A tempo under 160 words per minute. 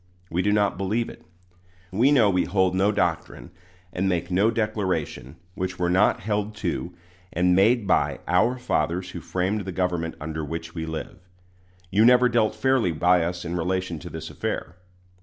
No: average, 175 wpm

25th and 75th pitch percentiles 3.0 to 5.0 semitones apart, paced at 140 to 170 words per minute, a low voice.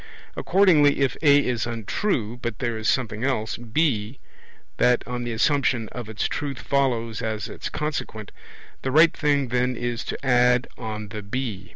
Yes: average, 3.8 semitones; average, 165 wpm; low, 125 Hz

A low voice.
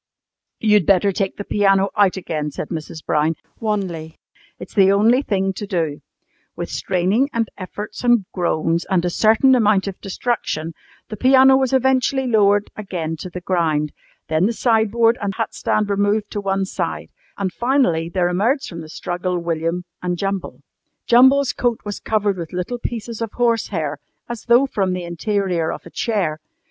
No: high, 200 Hz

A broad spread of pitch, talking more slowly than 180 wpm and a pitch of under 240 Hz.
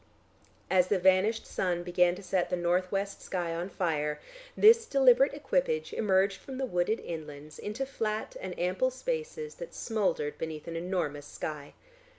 Yes: wide, 6.5 semitones; average, 160 wpm; high, 190 Hz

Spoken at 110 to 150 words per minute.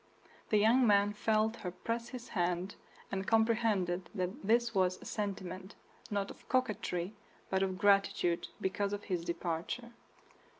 Yes: average, 140 wpm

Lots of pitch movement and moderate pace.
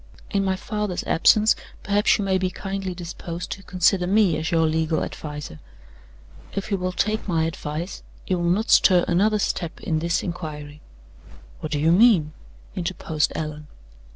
No: average, 3.5 semitones; average, 160 wpm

